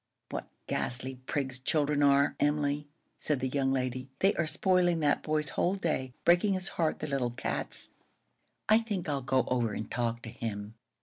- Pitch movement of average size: Yes, average, 4.0 semitones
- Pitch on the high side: No, medium, 140 Hz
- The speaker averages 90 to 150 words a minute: No, average, 175 wpm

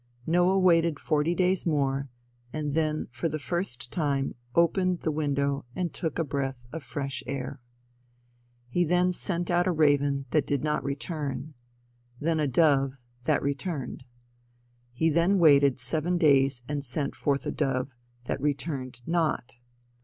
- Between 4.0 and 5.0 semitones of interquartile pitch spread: No, average, 3.4 semitones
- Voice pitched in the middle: Yes, medium, 150 Hz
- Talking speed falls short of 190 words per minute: Yes, average, 145 wpm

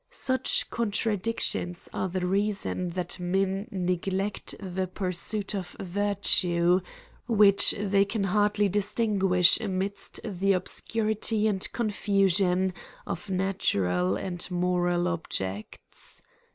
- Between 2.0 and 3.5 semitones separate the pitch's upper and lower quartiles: Yes, narrow, 2.4 semitones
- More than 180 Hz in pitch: Yes, high, 190 Hz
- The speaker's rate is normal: No, slow, 105 wpm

